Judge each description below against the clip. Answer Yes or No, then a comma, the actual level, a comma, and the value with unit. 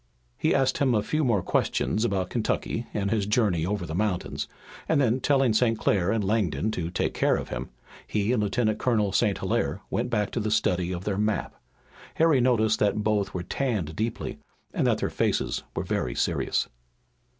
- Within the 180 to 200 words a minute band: Yes, average, 190 wpm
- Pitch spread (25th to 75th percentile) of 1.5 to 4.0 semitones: Yes, average, 3.5 semitones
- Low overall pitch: Yes, low, 105 Hz